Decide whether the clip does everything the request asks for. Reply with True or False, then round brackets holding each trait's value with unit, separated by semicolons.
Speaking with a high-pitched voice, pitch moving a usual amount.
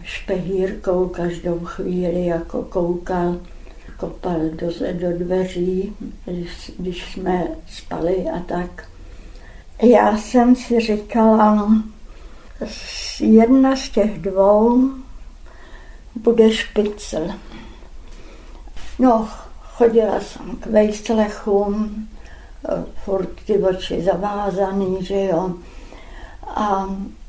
True (195 Hz; 3.5 semitones)